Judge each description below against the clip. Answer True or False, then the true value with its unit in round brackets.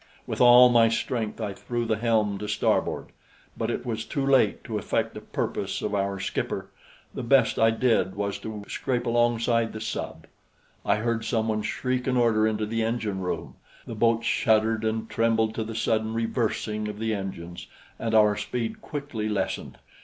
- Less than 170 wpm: False (175 wpm)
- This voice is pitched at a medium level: False (110 Hz)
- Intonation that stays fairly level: True (1.6 semitones)